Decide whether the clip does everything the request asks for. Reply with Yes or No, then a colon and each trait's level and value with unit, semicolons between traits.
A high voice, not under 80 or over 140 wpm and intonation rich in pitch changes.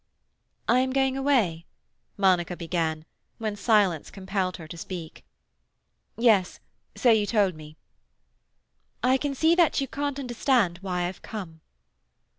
Yes: high, 200 Hz; slow, 135 wpm; wide, 6.6 semitones